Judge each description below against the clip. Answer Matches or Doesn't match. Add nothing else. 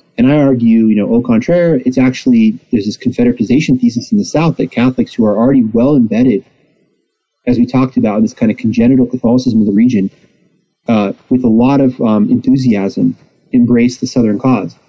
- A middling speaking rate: Matches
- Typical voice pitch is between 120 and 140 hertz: Matches